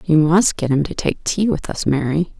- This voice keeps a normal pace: No, fast, 250 wpm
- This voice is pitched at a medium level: Yes, medium, 160 Hz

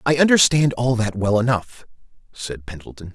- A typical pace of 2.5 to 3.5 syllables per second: No, 5.0 syllables/s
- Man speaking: Yes, male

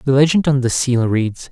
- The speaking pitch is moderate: No, low, 130 Hz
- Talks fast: Yes, fast, 235 wpm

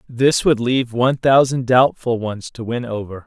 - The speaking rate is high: No, average, 185 wpm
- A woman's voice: No, male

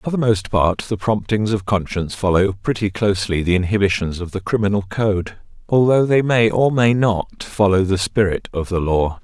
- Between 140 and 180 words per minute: No, average, 190 wpm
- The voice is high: No, low, 100 Hz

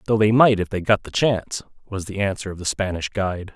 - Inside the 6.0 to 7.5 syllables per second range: Yes, 6.1 syllables/s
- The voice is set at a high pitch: No, low, 100 Hz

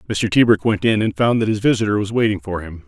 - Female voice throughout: No, male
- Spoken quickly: Yes, fast, 270 wpm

